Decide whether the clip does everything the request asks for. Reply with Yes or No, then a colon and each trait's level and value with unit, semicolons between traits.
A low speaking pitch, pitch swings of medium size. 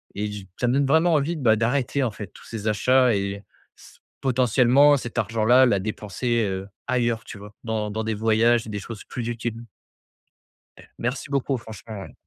Yes: low, 115 Hz; average, 3.1 semitones